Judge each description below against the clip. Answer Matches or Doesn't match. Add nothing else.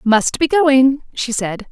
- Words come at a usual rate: Matches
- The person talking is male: Doesn't match